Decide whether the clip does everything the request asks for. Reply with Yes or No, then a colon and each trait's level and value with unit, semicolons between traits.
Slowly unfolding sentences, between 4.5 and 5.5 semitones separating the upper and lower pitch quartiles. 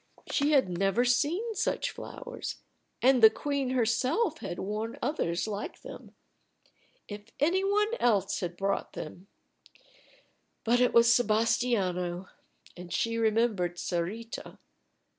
Yes: slow, 120 wpm; average, 5.0 semitones